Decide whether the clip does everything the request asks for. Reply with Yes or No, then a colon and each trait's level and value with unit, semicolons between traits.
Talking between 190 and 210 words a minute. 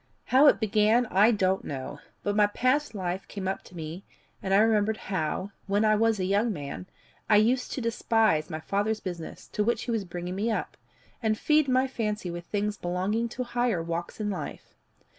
Yes: average, 200 wpm